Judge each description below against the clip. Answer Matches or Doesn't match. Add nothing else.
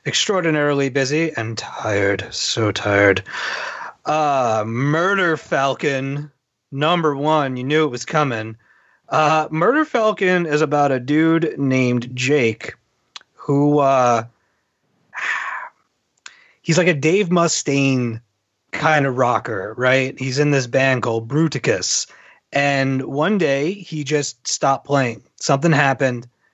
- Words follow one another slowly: Matches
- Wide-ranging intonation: Doesn't match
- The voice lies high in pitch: Doesn't match